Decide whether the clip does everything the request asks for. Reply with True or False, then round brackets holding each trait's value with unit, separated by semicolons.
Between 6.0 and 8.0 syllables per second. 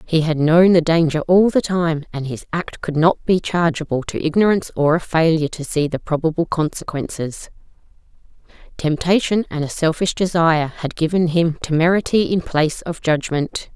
False (5.1 syllables/s)